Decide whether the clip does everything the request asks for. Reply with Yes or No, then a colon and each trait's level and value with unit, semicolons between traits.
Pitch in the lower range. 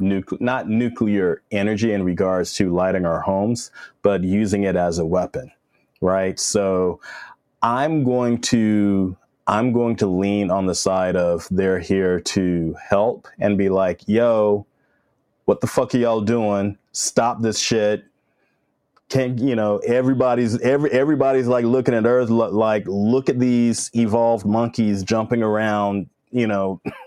Yes: low, 105 Hz